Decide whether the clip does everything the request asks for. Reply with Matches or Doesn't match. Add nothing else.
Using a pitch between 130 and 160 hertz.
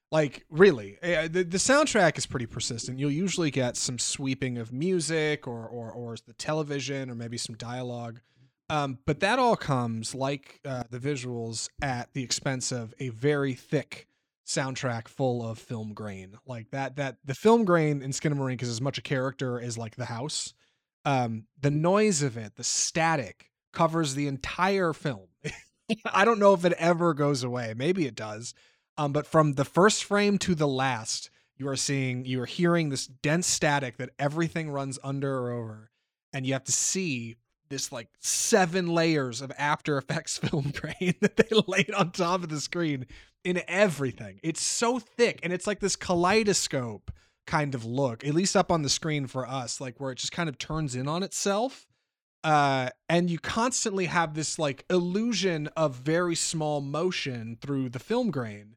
Matches